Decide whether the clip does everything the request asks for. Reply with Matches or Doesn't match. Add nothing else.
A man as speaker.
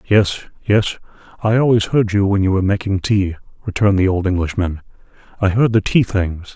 Matches